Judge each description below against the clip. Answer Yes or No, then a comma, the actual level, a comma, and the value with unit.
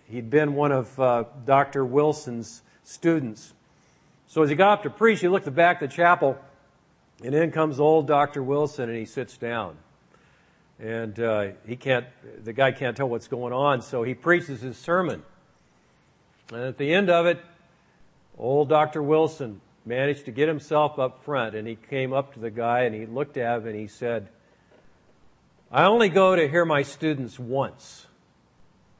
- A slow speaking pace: No, average, 180 wpm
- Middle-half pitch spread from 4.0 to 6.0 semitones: Yes, average, 4.3 semitones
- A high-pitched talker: No, low, 135 Hz